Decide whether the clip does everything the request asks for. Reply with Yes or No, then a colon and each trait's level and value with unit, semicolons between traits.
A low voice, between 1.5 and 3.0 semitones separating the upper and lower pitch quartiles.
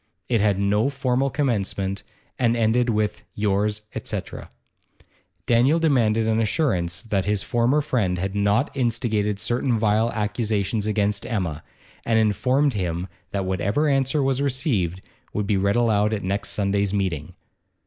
No: low, 105 Hz; average, 3.6 semitones